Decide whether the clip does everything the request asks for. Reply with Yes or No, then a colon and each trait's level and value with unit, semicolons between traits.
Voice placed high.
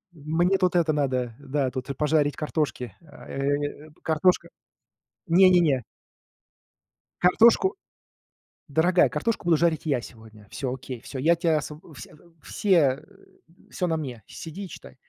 No: medium, 150 Hz